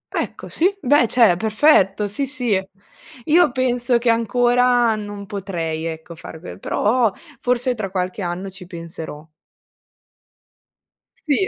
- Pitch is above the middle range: Yes, high, 215 Hz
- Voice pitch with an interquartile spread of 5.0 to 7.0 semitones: Yes, wide, 5.4 semitones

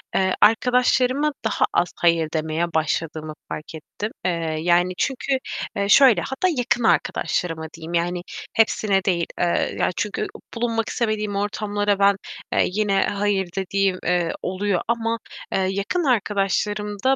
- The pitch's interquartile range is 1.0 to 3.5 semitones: No, average, 4.2 semitones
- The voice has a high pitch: Yes, high, 200 Hz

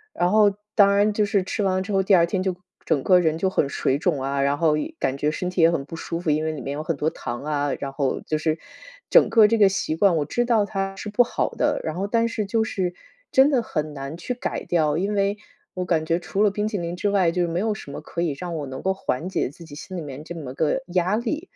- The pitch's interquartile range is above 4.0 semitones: Yes, average, 4.8 semitones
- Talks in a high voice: No, medium, 175 Hz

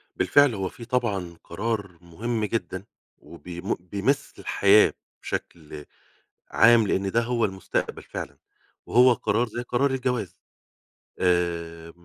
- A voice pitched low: Yes, low, 100 Hz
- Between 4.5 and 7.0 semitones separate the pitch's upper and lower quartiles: Yes, average, 5.2 semitones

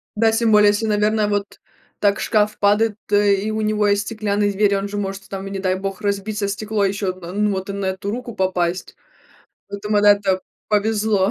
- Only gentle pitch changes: Yes, narrow, 1.3 semitones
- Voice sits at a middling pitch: No, high, 205 Hz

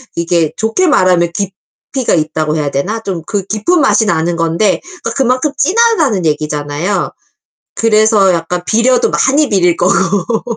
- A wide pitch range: Yes, wide, 6.0 semitones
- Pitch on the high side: Yes, high, 195 Hz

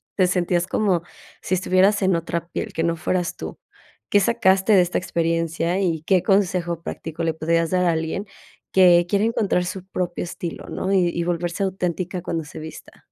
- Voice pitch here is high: No, medium, 175 Hz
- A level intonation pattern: Yes, narrow, 2.0 semitones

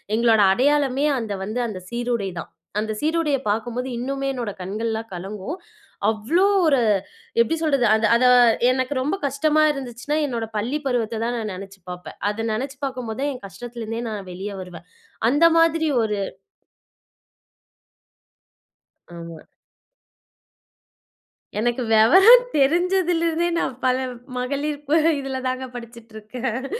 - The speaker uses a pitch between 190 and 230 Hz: No, high, 245 Hz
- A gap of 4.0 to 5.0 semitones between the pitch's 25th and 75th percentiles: Yes, average, 4.5 semitones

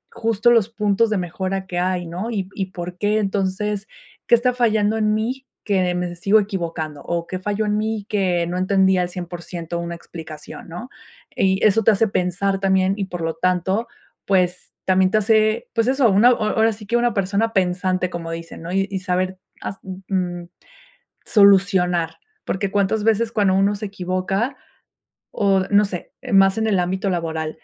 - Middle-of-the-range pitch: No, high, 195 Hz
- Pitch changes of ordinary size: Yes, average, 3.0 semitones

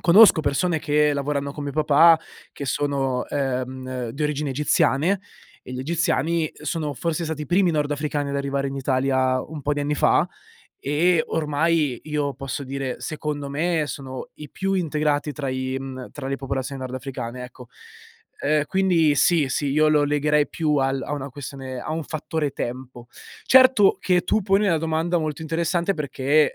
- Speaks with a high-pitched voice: No, medium, 145 Hz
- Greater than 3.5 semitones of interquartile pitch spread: No, average, 2.9 semitones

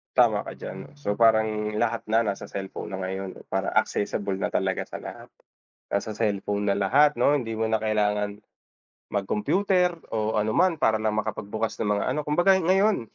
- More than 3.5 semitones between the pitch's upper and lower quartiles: No, narrow, 2.6 semitones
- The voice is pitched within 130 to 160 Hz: No, low, 110 Hz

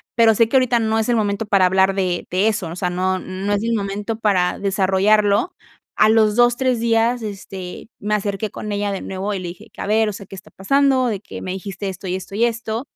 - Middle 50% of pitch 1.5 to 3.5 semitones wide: Yes, average, 2.8 semitones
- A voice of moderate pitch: No, high, 205 Hz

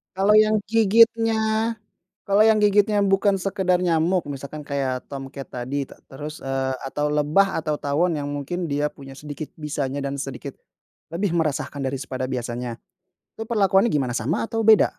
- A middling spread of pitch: No, wide, 6.3 semitones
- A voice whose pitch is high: No, medium, 150 Hz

